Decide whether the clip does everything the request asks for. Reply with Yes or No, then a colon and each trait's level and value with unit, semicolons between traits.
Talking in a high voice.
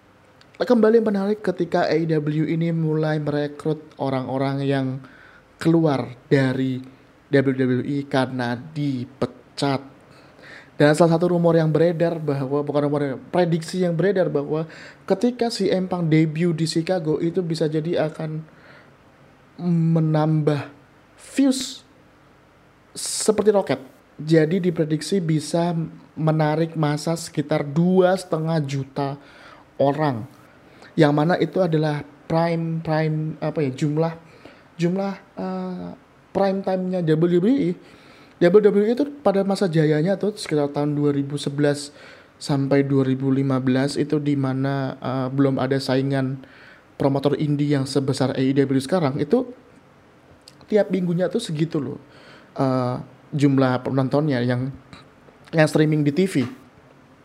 No: medium, 150 Hz